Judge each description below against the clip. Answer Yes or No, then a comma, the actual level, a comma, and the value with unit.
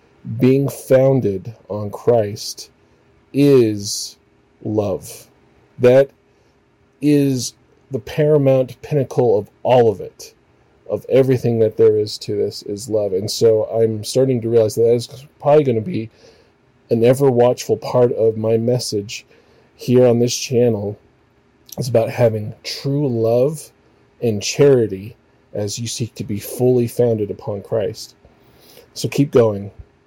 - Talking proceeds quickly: No, slow, 135 wpm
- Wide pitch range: No, average, 3.6 semitones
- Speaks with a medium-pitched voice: No, low, 120 Hz